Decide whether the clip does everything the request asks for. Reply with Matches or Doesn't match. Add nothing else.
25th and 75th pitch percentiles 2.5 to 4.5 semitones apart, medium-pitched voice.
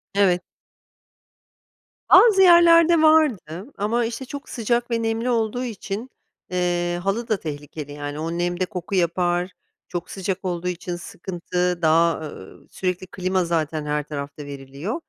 Doesn't match